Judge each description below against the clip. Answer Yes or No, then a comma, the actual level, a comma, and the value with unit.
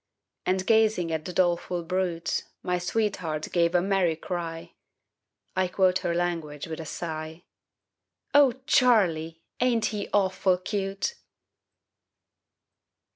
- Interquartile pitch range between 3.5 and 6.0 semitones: No, average, 2.9 semitones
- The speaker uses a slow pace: Yes, slow, 115 wpm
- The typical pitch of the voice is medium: Yes, medium, 180 Hz